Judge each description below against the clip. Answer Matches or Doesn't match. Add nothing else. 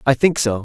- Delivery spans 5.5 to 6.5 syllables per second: Matches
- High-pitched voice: Doesn't match